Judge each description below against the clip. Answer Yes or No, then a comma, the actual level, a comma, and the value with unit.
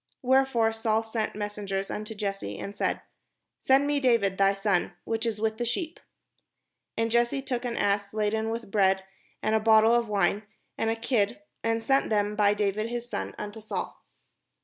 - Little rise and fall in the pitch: Yes, narrow, 2.3 semitones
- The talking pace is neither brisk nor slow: Yes, average, 175 wpm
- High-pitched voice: Yes, high, 220 Hz